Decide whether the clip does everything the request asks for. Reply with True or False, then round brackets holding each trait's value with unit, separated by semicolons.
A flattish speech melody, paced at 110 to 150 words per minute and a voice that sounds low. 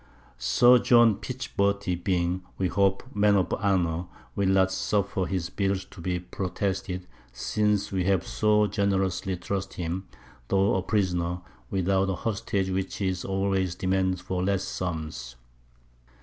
True (1.7 semitones; 140 wpm; 95 Hz)